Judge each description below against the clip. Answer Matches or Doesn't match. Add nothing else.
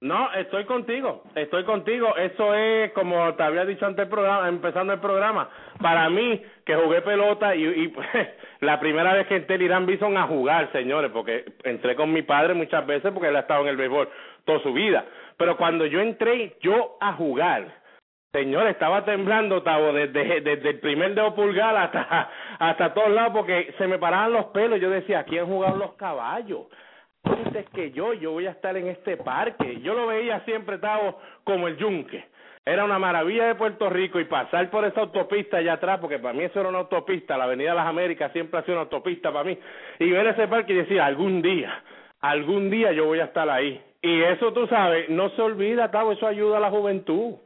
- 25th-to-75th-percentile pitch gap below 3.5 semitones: Doesn't match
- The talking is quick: Matches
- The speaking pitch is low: Doesn't match